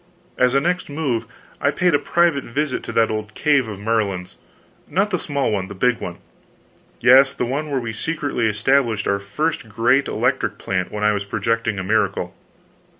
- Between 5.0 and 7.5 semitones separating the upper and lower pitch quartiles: Yes, average, 5.3 semitones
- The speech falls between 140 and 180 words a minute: No, average, 190 wpm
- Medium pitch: No, low, 120 Hz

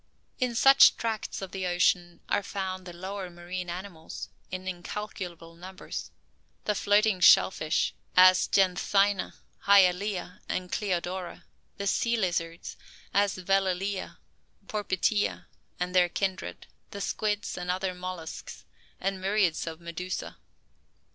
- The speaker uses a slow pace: Yes, slow, 120 wpm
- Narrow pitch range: Yes, narrow, 2.1 semitones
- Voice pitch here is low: No, medium, 185 Hz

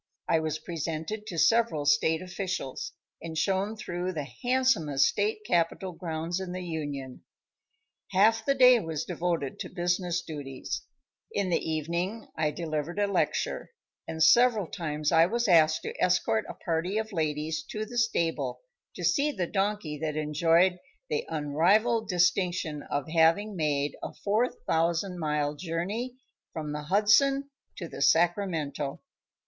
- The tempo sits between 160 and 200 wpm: No, average, 140 wpm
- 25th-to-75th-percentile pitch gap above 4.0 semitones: Yes, average, 4.5 semitones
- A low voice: No, medium, 170 Hz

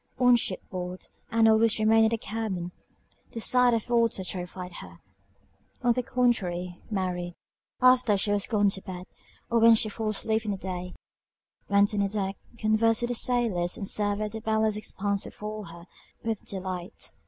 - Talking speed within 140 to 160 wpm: No, average, 175 wpm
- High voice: Yes, high, 210 Hz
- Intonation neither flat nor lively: Yes, average, 3.3 semitones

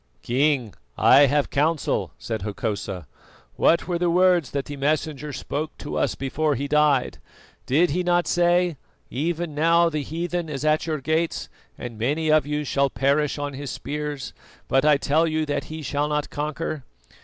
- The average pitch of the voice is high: No, medium, 150 Hz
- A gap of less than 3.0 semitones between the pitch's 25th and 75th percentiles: Yes, narrow, 2.5 semitones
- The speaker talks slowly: No, average, 170 wpm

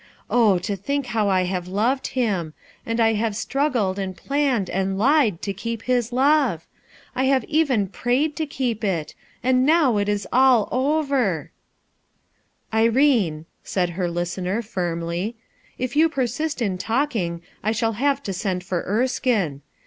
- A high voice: Yes, high, 225 Hz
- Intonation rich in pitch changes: Yes, wide, 5.7 semitones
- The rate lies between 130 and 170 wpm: Yes, average, 160 wpm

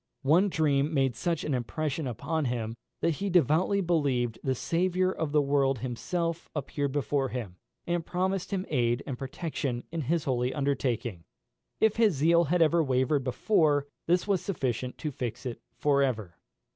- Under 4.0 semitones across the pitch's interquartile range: No, average, 4.8 semitones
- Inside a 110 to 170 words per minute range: Yes, average, 165 wpm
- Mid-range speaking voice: Yes, medium, 145 Hz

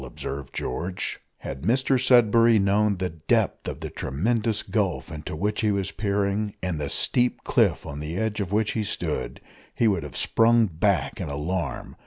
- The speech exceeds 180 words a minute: No, average, 175 wpm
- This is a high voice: No, low, 100 Hz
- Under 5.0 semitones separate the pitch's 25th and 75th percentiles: No, average, 5.3 semitones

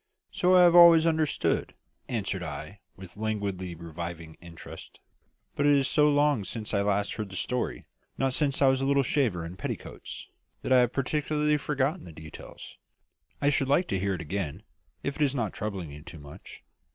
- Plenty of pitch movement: Yes, wide, 8.2 semitones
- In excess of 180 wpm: Yes, average, 190 wpm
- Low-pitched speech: Yes, low, 110 Hz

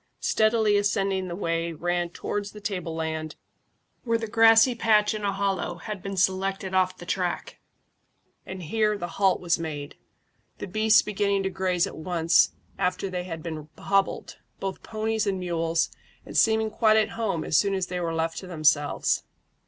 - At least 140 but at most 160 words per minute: No, average, 175 wpm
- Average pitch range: Yes, average, 3.5 semitones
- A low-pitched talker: No, high, 190 Hz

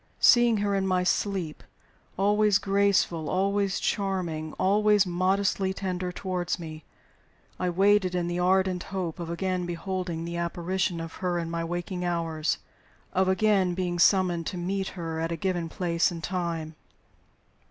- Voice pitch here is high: No, medium, 180 Hz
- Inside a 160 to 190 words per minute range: No, average, 150 wpm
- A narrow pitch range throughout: Yes, narrow, 2.2 semitones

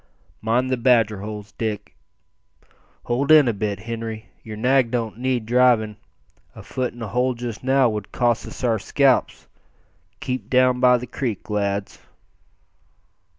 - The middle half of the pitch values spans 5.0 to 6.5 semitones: No, average, 2.7 semitones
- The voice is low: Yes, low, 120 Hz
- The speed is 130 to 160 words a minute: Yes, average, 150 wpm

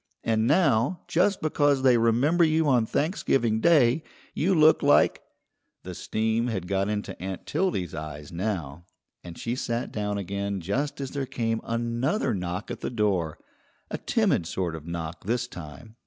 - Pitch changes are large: Yes, wide, 6.7 semitones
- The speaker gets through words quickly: No, average, 165 wpm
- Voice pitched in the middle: No, low, 115 Hz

